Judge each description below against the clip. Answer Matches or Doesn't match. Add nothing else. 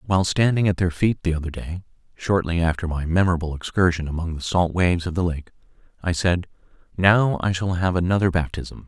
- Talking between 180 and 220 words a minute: Matches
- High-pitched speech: Doesn't match